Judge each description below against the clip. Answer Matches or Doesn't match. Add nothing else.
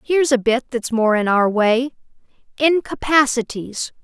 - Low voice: Doesn't match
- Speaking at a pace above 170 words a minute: Doesn't match